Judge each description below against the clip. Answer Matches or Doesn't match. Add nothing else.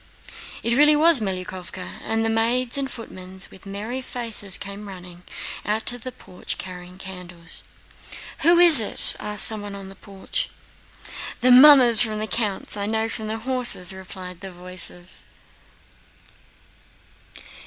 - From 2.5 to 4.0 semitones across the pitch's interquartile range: Doesn't match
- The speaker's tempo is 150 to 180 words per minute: Doesn't match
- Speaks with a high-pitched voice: Matches